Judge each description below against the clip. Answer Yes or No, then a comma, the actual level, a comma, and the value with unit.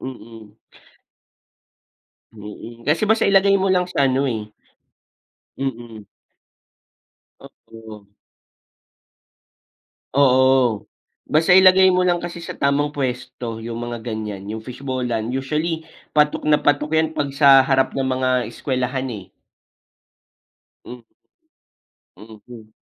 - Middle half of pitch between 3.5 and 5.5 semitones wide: Yes, average, 4.7 semitones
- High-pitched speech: No, low, 130 Hz